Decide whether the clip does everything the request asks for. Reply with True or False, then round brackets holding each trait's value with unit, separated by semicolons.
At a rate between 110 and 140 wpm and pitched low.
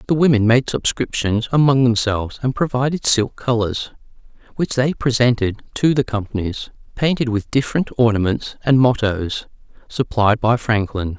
True (135 wpm; 120 Hz)